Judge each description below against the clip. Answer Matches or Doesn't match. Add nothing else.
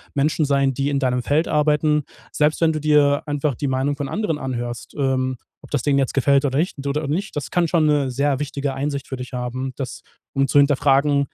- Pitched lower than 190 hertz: Matches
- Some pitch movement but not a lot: Doesn't match